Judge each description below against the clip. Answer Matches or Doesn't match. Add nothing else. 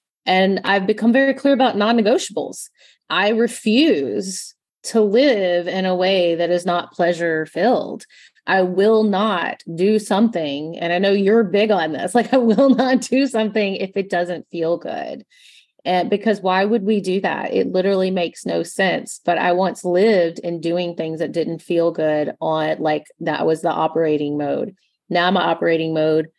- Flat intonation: Doesn't match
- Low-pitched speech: Doesn't match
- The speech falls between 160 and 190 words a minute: Matches